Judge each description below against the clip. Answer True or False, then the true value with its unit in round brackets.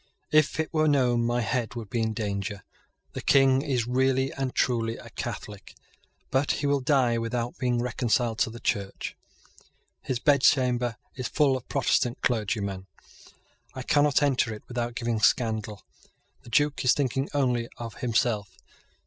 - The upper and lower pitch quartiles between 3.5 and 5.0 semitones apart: False (2.7 semitones)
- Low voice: True (120 Hz)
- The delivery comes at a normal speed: True (155 wpm)